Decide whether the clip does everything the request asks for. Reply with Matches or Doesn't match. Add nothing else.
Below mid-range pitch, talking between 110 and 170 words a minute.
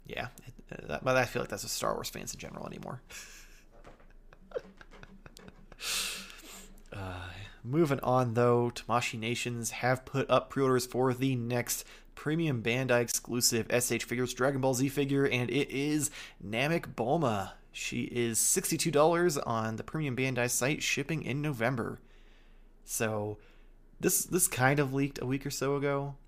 Matches